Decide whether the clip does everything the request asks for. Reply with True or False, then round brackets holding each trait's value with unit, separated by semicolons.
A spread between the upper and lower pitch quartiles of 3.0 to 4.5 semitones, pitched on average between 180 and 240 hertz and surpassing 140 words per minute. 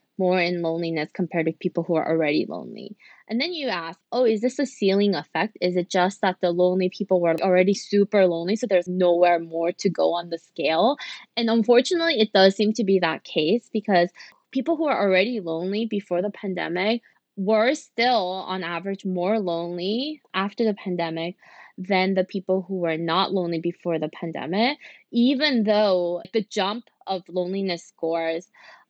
True (3.9 semitones; 190 Hz; 175 wpm)